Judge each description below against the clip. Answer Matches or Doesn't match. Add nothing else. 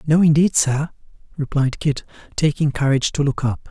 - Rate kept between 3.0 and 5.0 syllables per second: Doesn't match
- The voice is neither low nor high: Matches